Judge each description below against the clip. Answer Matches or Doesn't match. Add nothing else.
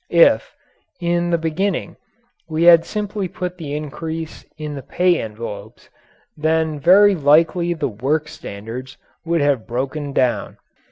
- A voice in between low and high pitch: Matches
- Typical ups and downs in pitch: Matches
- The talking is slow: Matches